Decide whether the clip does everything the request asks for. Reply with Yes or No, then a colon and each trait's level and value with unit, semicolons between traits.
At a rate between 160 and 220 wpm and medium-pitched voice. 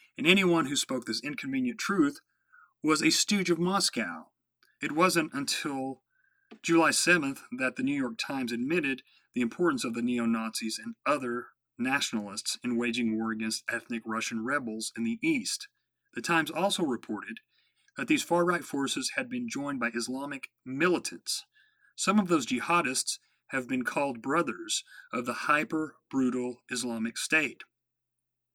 No: average, 150 wpm; medium, 150 Hz